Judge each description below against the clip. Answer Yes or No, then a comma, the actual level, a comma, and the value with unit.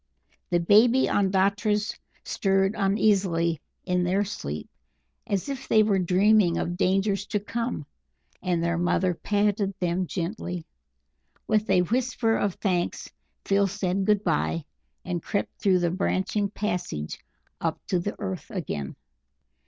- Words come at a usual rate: No, slow, 130 wpm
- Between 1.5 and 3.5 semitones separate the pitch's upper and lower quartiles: Yes, average, 2.7 semitones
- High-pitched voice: Yes, high, 195 Hz